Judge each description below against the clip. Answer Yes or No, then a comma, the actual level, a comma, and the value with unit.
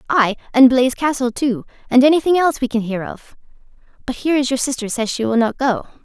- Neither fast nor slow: No, fast, 220 wpm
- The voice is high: Yes, very high, 255 Hz